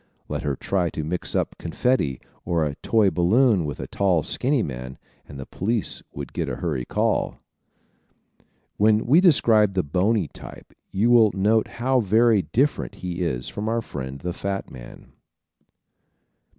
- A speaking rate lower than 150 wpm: No, average, 160 wpm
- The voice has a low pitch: Yes, very low, 95 Hz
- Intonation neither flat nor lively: No, wide, 6.5 semitones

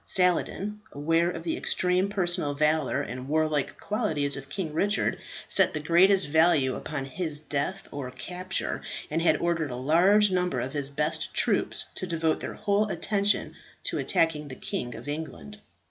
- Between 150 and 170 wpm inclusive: Yes, average, 160 wpm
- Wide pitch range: No, average, 4.1 semitones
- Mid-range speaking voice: Yes, medium, 160 Hz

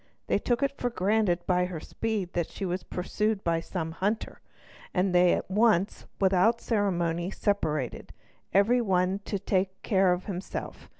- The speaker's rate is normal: Yes, average, 160 wpm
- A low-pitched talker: No, high, 190 Hz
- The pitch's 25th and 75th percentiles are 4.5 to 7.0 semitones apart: No, average, 2.9 semitones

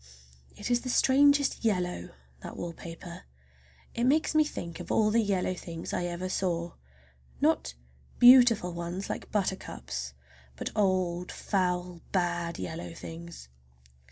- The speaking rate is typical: No, slow, 125 wpm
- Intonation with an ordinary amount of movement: Yes, average, 4.0 semitones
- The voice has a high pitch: No, medium, 180 Hz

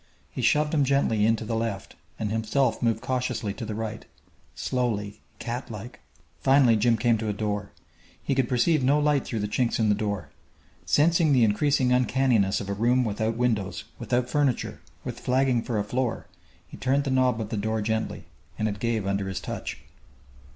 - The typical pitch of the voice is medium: No, low, 115 Hz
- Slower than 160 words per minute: No, average, 185 wpm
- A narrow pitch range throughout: No, average, 3.3 semitones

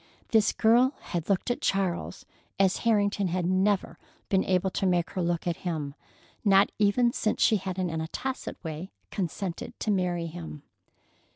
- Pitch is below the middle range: No, high, 190 Hz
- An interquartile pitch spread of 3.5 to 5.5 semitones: No, average, 2.9 semitones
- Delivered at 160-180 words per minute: Yes, average, 165 wpm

